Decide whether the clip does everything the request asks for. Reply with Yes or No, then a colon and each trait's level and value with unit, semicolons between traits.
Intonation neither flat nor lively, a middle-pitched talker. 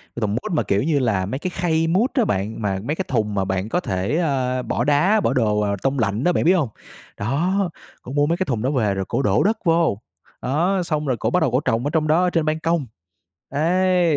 No: wide, 7.3 semitones; medium, 145 Hz